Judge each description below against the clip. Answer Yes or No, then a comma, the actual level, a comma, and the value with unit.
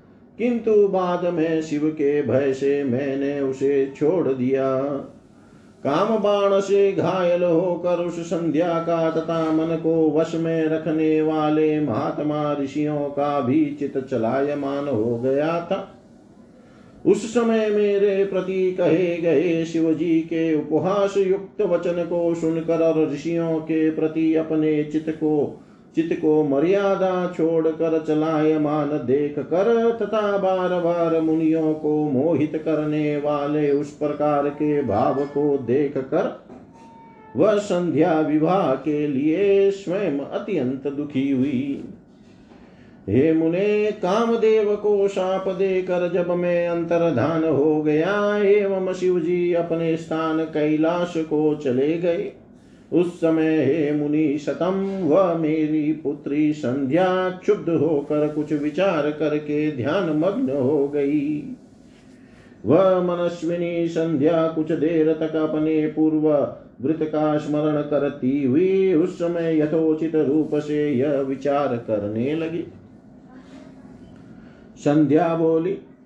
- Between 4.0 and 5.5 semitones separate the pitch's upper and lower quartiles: No, average, 3.1 semitones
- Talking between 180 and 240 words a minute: No, average, 120 wpm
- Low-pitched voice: No, medium, 160 Hz